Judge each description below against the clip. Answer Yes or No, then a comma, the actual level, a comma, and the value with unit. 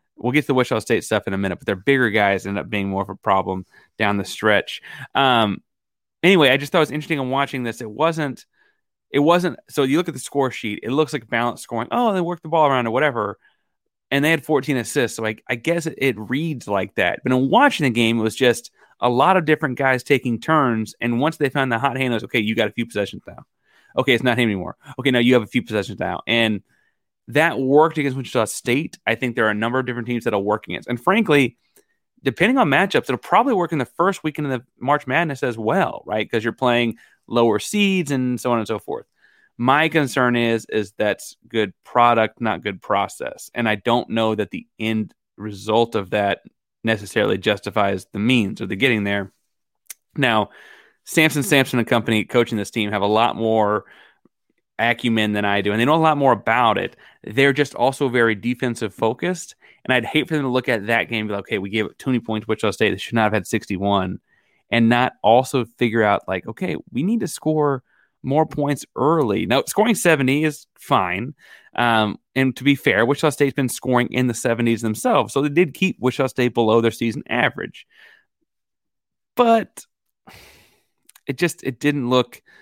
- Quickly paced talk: Yes, fast, 215 wpm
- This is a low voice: Yes, low, 125 Hz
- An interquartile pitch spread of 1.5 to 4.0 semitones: No, average, 4.5 semitones